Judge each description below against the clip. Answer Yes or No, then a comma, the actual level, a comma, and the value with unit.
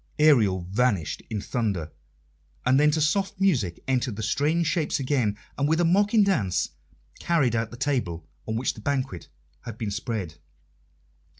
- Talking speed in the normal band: Yes, average, 160 wpm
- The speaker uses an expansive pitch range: Yes, wide, 6.4 semitones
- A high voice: No, low, 125 Hz